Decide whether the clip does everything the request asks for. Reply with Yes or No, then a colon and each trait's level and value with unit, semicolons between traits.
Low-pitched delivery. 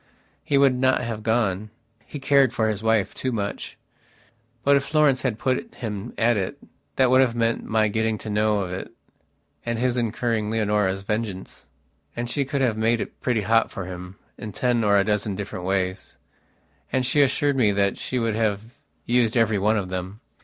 Yes: low, 110 Hz